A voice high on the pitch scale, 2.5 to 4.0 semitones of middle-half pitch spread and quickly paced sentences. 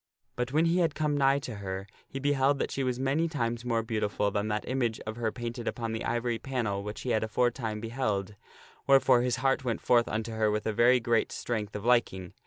No: low, 120 Hz; average, 3.4 semitones; fast, 220 wpm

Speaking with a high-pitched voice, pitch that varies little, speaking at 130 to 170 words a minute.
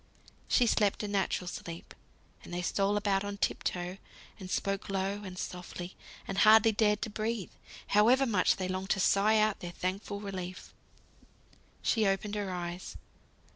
Yes: high, 195 Hz; narrow, 2.2 semitones; average, 160 wpm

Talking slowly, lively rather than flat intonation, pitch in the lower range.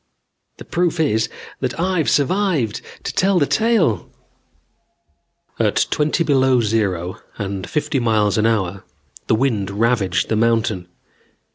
Yes: slow, 125 wpm; wide, 7.1 semitones; low, 115 Hz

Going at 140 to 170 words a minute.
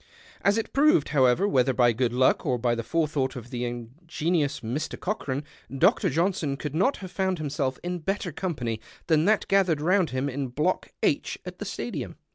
No: average, 185 wpm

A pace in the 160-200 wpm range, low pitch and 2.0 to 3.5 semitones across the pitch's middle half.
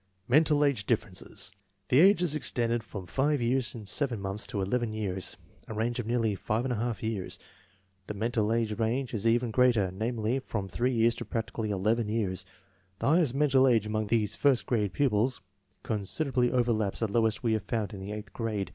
Yes: average, 175 wpm; low, 115 Hz; average, 2.9 semitones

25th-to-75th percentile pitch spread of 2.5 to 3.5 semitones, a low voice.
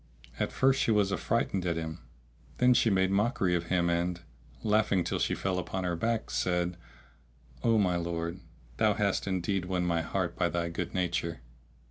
Yes: average, 2.8 semitones; very low, 90 Hz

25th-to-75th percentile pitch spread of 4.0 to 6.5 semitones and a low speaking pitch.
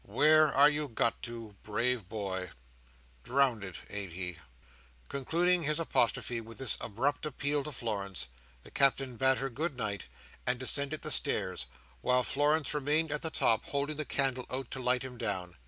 Yes: average, 4.4 semitones; low, 130 Hz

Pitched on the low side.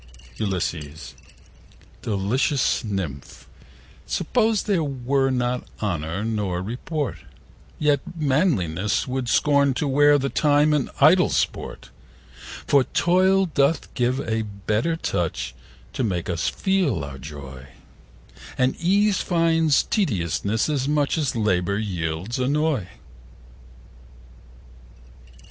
Yes: low, 125 Hz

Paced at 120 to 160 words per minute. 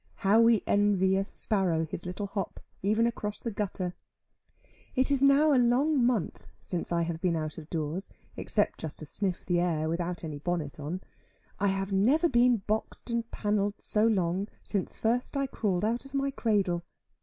No: average, 180 wpm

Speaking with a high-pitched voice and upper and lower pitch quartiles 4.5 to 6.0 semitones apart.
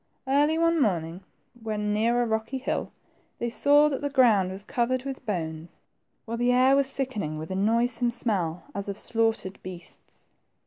Yes: high, 230 Hz; average, 5.0 semitones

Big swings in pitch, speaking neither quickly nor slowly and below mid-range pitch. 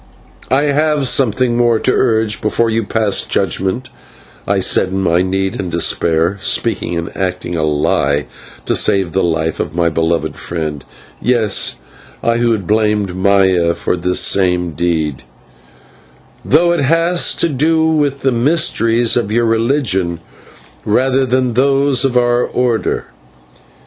Yes: wide, 6.3 semitones; average, 145 wpm; low, 110 Hz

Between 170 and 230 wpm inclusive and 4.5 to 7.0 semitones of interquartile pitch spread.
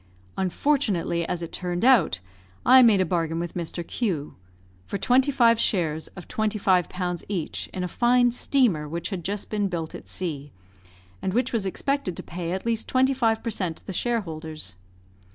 Yes: average, 180 wpm; wide, 5.5 semitones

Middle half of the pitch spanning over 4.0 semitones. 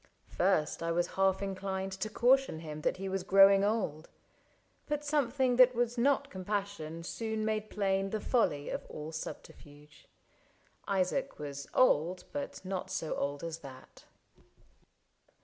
Yes: wide, 5.5 semitones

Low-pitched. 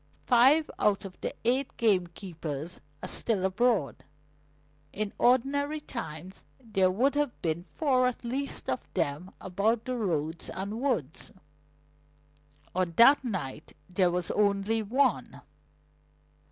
No: high, 205 Hz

